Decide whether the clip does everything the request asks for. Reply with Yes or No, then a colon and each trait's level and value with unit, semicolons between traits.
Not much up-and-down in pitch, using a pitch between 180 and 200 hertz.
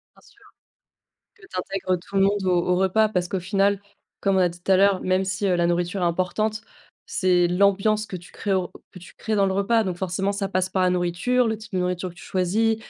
Yes: narrow, 1.9 semitones; high, 190 Hz